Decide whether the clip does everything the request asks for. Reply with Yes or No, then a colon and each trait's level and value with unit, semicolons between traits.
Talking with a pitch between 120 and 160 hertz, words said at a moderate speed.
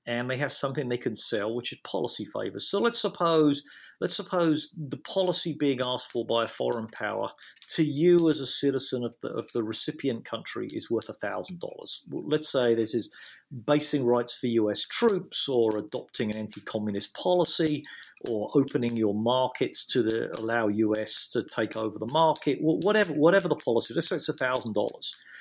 Yes: low, 135 Hz; average, 180 wpm